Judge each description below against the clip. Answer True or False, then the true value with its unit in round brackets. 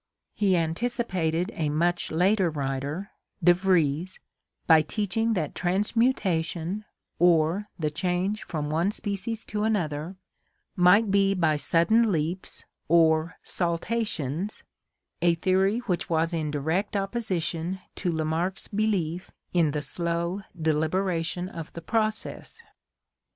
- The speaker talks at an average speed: False (120 wpm)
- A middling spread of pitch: True (3.8 semitones)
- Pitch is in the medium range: True (175 Hz)